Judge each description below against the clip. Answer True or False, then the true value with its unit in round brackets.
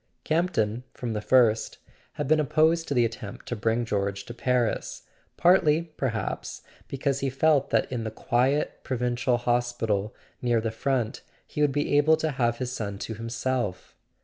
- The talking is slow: False (170 wpm)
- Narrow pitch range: False (3.8 semitones)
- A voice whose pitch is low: True (125 Hz)